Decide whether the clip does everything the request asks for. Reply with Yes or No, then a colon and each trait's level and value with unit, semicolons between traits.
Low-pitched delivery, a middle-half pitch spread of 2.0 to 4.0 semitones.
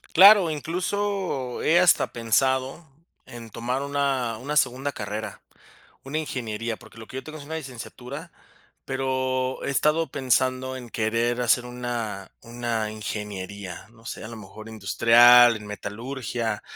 Yes: low, 125 Hz; average, 3.5 semitones